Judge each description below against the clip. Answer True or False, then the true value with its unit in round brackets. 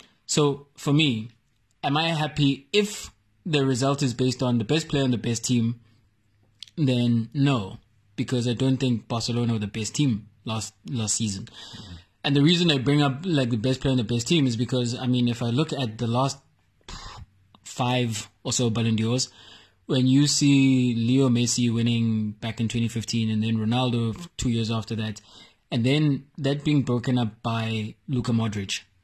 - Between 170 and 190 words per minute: True (180 wpm)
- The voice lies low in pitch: True (120 Hz)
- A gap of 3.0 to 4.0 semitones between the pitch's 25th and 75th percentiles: True (3.4 semitones)